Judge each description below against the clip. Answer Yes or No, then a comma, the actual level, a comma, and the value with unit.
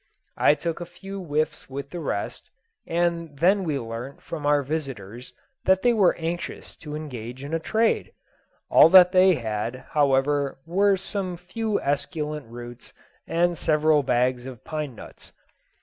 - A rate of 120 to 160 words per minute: Yes, average, 150 wpm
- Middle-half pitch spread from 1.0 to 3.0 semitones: No, average, 4.7 semitones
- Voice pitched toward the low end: No, medium, 150 Hz